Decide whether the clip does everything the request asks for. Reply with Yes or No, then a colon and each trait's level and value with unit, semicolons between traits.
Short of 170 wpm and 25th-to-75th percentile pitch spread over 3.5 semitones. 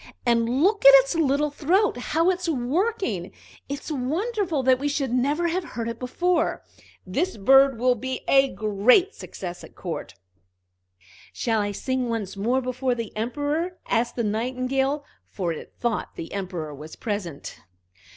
Yes: average, 150 wpm; average, 5.2 semitones